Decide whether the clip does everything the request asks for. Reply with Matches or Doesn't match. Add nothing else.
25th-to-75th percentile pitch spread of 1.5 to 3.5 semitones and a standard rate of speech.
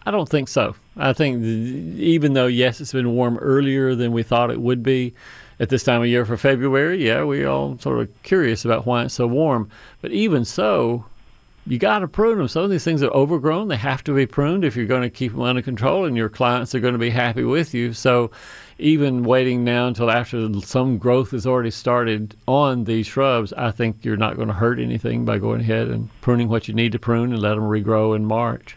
Doesn't match